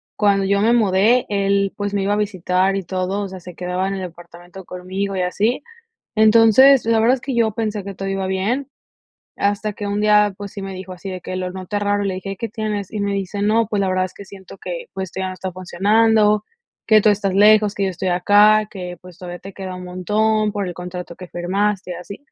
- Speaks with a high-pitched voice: Yes, high, 200 Hz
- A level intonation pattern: Yes, narrow, 2.2 semitones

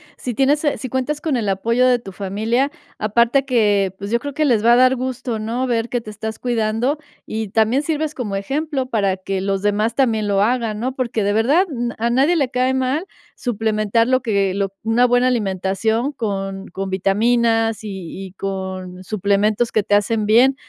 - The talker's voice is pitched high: Yes, high, 225 Hz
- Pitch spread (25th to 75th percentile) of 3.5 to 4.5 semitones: Yes, average, 4.0 semitones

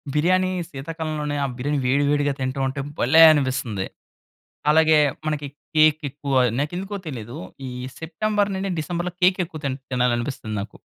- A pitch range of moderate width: Yes, average, 3.6 semitones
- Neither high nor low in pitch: Yes, medium, 150 Hz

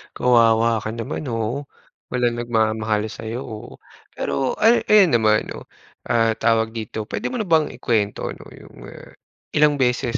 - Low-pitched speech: Yes, low, 115 Hz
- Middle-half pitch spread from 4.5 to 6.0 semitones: No, average, 2.9 semitones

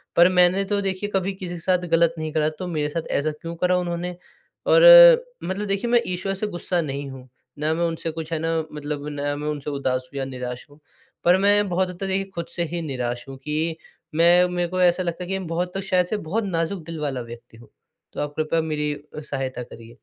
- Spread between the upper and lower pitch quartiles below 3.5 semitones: No, average, 3.8 semitones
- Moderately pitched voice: Yes, medium, 165 Hz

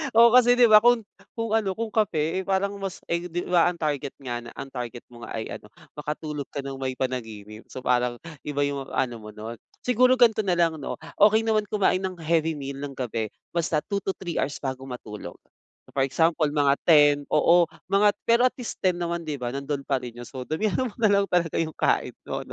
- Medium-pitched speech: Yes, medium, 155 Hz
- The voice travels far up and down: Yes, wide, 6.9 semitones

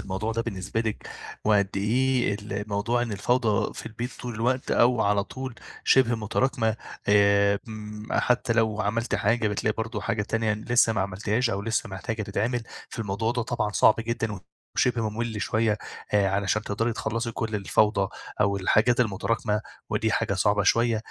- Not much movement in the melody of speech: Yes, narrow, 2.2 semitones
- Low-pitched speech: Yes, low, 110 Hz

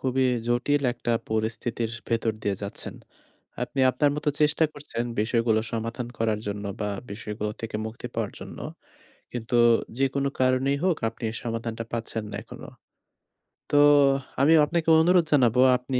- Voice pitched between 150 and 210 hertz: No, low, 120 Hz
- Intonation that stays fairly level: No, average, 3.6 semitones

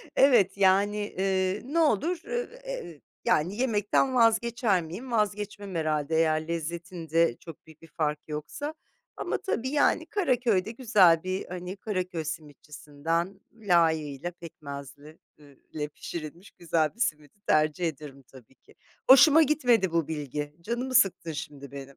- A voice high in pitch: No, medium, 175 Hz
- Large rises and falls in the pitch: Yes, wide, 6.0 semitones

